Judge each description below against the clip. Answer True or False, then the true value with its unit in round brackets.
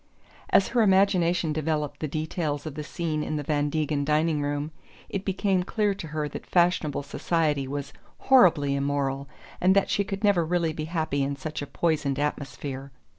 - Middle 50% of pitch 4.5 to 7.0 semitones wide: False (3.5 semitones)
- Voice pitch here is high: False (155 Hz)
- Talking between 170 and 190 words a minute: True (175 wpm)